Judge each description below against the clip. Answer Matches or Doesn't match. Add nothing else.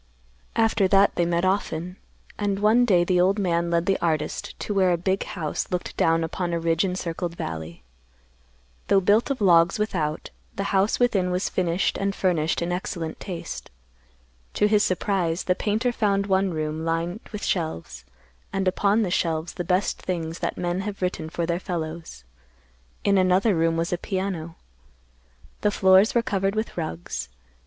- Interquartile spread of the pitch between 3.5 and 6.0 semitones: Doesn't match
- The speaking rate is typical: Matches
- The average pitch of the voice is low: Doesn't match